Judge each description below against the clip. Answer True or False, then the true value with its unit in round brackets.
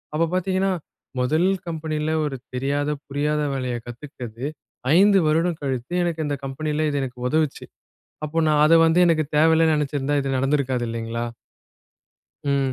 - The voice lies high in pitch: False (150 Hz)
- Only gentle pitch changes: False (3.2 semitones)